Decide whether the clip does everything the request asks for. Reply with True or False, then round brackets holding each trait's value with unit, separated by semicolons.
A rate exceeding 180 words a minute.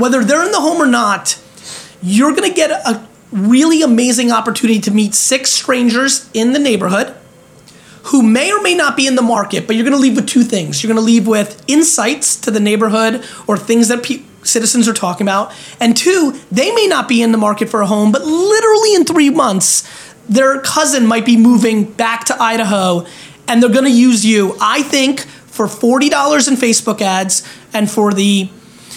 True (195 wpm)